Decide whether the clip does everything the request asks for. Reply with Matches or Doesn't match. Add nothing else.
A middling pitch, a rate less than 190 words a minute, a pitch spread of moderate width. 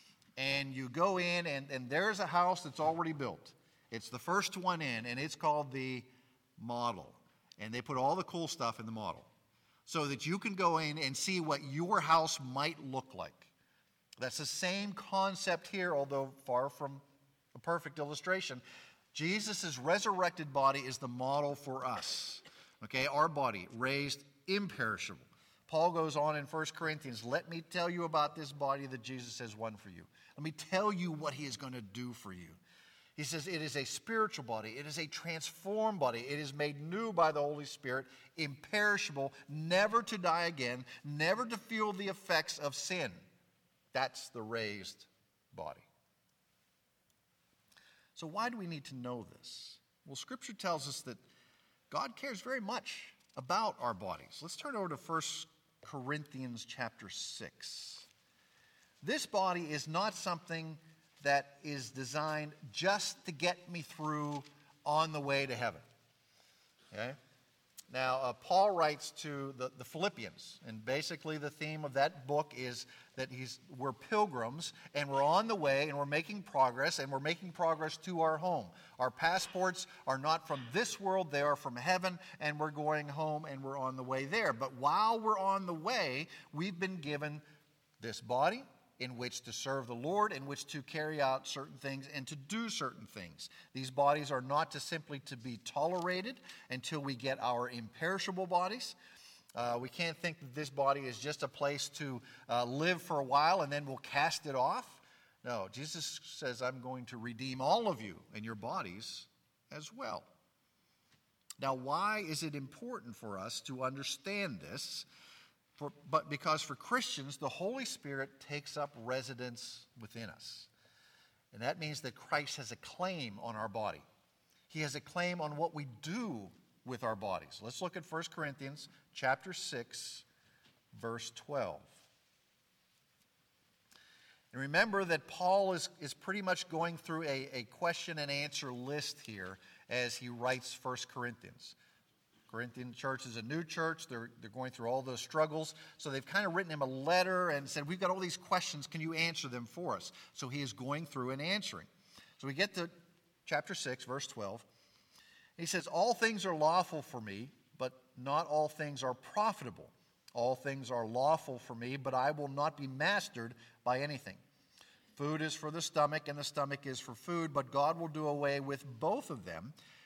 Matches